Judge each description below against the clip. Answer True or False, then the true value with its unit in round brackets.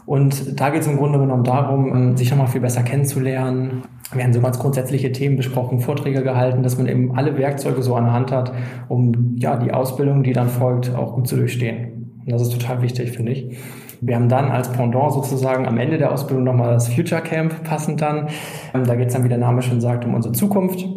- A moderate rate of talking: False (225 wpm)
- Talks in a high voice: False (130 Hz)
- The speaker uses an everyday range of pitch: False (2.0 semitones)